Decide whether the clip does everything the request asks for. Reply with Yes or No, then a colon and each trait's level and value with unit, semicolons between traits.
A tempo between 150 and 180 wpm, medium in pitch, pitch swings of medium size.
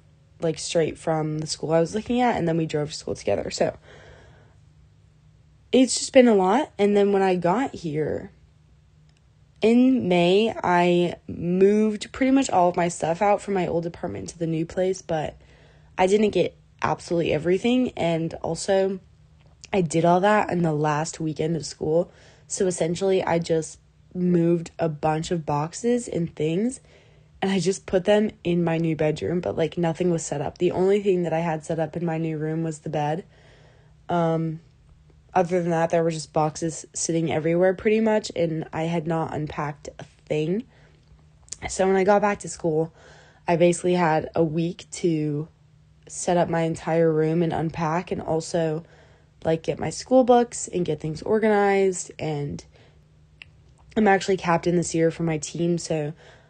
Yes: average, 175 wpm; medium, 170 Hz; average, 3.1 semitones